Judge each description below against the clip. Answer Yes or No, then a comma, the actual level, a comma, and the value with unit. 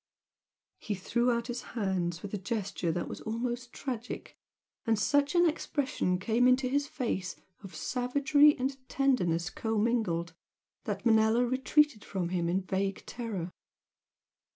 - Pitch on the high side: Yes, high, 230 Hz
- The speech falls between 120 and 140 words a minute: Yes, slow, 135 wpm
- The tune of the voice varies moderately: Yes, average, 5.0 semitones